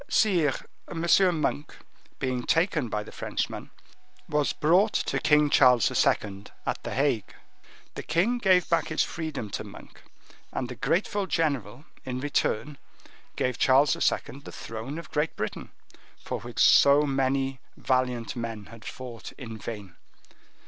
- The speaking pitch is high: No, low, 135 Hz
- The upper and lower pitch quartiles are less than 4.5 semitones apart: No, average, 4.8 semitones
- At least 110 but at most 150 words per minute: Yes, average, 140 wpm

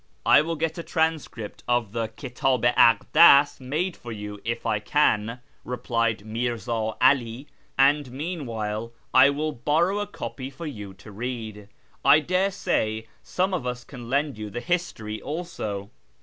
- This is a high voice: No, low, 125 Hz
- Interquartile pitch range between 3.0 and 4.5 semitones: No, average, 5.3 semitones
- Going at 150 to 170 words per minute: Yes, average, 160 wpm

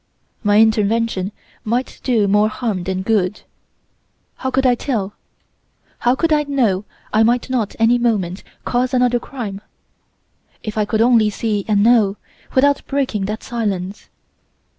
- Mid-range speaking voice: No, high, 225 Hz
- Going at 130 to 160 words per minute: Yes, average, 140 wpm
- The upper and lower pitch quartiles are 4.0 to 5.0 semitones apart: No, average, 3.1 semitones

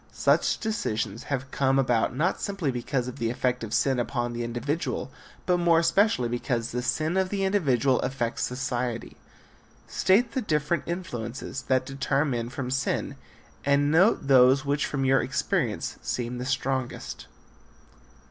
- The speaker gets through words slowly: No, average, 150 wpm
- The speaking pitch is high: No, low, 135 Hz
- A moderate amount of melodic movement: Yes, average, 4.2 semitones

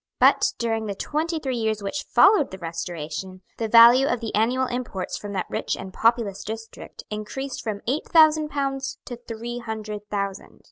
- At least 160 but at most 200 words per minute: Yes, average, 175 wpm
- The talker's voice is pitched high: Yes, high, 225 Hz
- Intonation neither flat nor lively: Yes, average, 4.6 semitones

